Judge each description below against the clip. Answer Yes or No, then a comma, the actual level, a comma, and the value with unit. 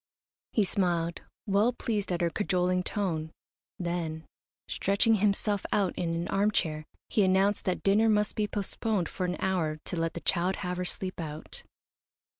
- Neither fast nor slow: Yes, average, 160 wpm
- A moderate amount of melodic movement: Yes, average, 3.1 semitones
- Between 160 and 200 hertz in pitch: Yes, medium, 185 Hz